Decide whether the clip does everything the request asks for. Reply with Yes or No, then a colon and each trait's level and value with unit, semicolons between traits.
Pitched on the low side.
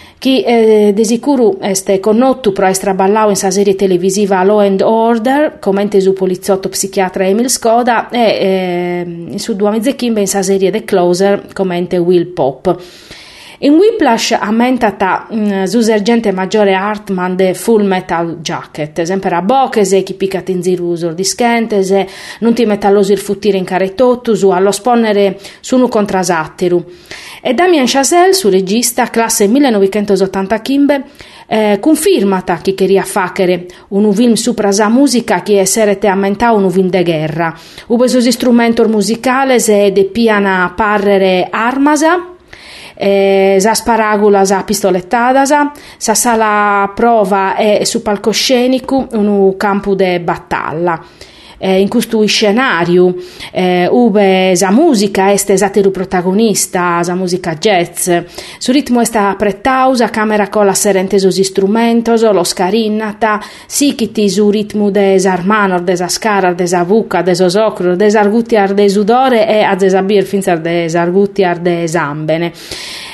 No: high, 200 Hz